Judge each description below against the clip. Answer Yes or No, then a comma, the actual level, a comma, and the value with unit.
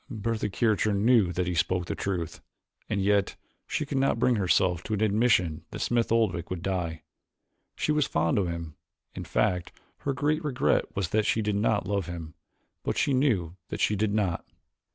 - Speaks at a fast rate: No, average, 195 wpm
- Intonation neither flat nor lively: Yes, average, 4.6 semitones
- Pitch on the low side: Yes, low, 100 Hz